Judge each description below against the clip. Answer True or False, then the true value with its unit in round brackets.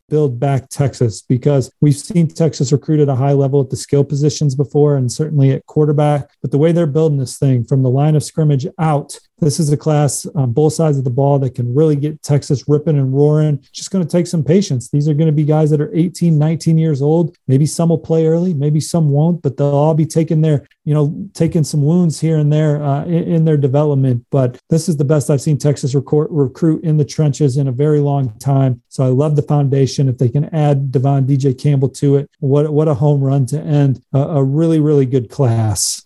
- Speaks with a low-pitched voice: False (145 Hz)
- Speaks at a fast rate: True (240 wpm)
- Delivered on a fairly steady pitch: True (2.1 semitones)